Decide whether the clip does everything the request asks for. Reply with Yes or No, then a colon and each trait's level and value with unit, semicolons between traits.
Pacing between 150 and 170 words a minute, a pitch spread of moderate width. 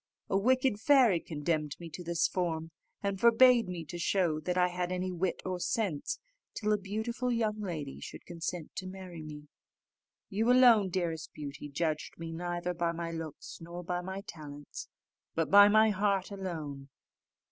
Yes: average, 165 wpm; average, 3.7 semitones